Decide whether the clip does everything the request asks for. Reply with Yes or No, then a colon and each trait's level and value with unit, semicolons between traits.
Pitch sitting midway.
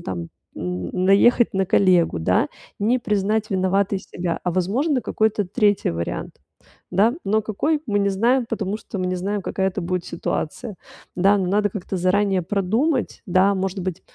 No: high, 195 Hz